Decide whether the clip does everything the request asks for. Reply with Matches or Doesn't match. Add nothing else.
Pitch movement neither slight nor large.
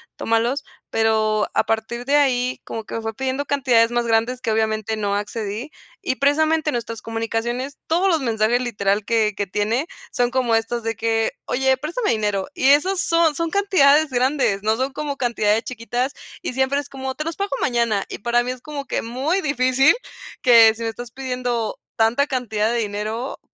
Matches